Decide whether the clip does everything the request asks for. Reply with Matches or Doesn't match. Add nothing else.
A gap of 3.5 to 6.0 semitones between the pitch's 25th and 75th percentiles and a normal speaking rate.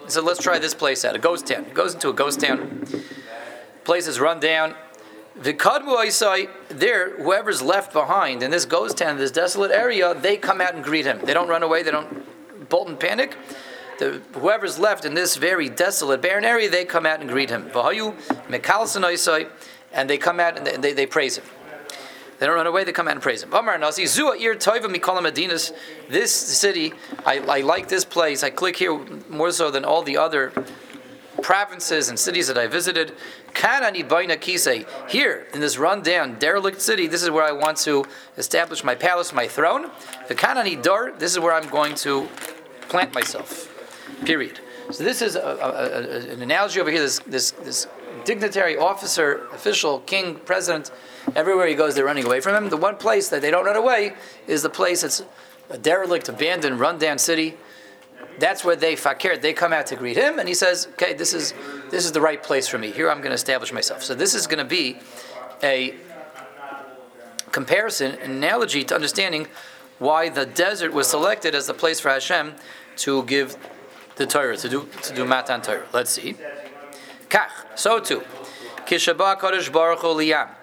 Matches